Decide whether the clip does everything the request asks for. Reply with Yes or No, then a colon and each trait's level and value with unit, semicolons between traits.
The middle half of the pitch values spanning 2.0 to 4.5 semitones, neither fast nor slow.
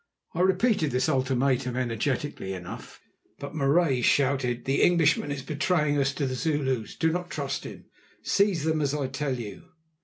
Yes: average, 3.6 semitones; average, 160 wpm